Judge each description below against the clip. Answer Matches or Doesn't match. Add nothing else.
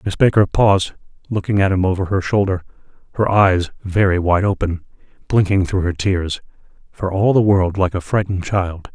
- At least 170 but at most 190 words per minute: Matches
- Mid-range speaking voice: Doesn't match